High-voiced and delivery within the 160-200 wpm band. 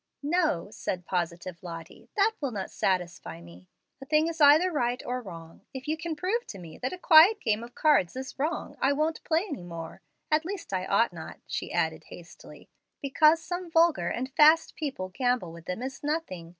Yes: very high, 265 Hz; average, 195 wpm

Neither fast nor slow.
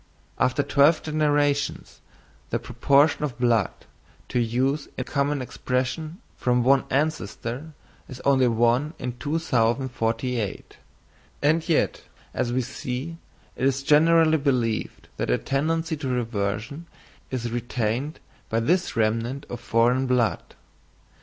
No: slow, 120 wpm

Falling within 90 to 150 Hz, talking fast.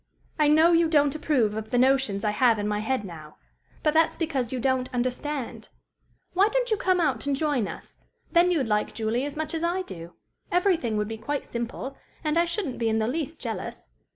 No: very high, 270 Hz; fast, 210 wpm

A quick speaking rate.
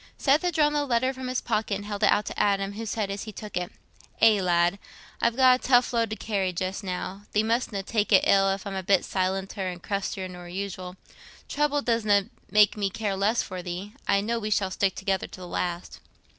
Yes: fast, 225 wpm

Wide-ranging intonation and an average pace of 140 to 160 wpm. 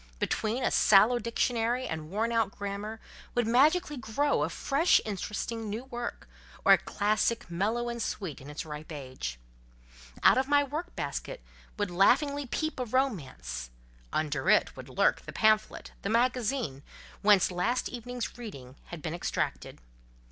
Yes: wide, 6.0 semitones; average, 150 wpm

